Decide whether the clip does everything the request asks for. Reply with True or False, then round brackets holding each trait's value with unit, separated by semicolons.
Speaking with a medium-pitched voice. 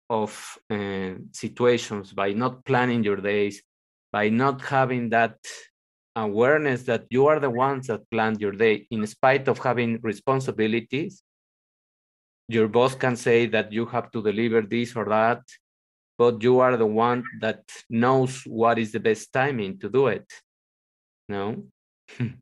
False (115 Hz)